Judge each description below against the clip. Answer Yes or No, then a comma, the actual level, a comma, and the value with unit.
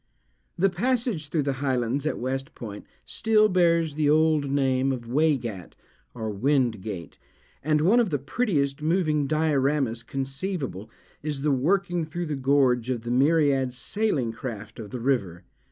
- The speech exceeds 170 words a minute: No, average, 155 wpm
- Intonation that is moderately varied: Yes, average, 4.3 semitones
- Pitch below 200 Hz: Yes, medium, 140 Hz